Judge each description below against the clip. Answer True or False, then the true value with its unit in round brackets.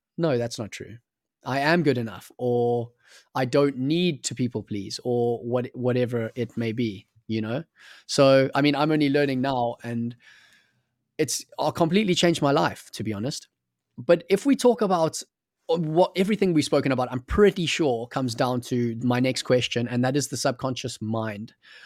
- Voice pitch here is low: True (130 Hz)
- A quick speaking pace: False (180 wpm)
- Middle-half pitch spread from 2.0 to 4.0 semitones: False (4.4 semitones)